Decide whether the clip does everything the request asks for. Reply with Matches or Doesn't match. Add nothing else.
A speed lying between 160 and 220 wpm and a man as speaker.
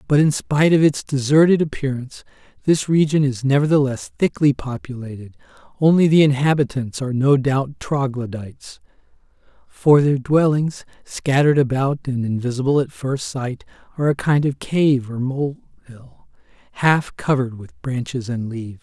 Doesn't match